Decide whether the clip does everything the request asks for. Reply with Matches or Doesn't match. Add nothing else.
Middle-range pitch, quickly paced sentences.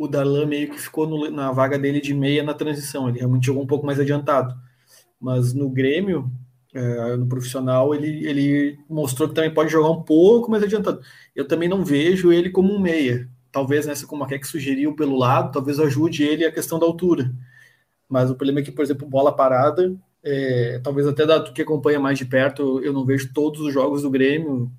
Matches